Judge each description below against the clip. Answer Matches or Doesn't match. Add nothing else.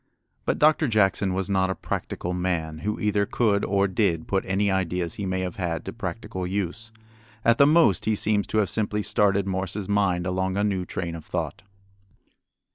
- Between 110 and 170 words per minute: Doesn't match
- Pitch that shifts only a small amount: Matches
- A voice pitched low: Matches